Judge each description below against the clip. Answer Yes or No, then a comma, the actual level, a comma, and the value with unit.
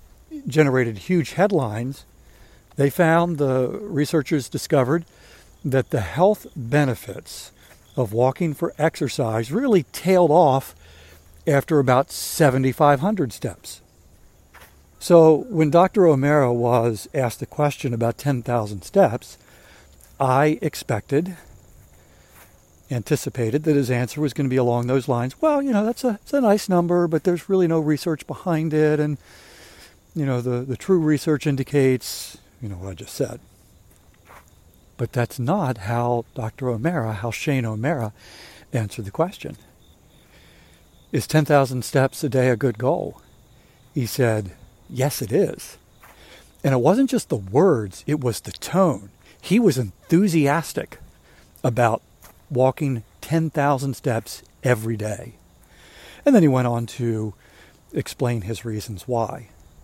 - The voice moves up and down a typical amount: No, wide, 5.8 semitones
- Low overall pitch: Yes, low, 130 Hz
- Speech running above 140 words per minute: No, slow, 135 wpm